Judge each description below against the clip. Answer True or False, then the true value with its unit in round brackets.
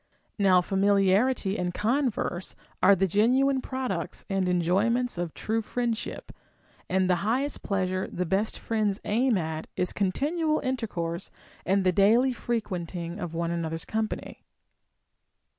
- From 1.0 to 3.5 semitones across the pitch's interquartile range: False (4.6 semitones)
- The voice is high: True (200 Hz)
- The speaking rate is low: True (125 wpm)